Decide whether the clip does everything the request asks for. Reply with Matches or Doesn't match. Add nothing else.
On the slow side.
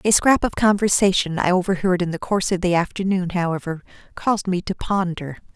Doesn't match